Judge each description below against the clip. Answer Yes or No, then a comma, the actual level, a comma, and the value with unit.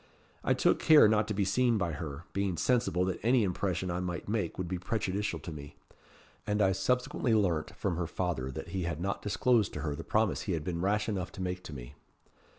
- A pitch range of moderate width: Yes, average, 3.7 semitones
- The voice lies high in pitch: No, very low, 95 Hz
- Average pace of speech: No, fast, 225 wpm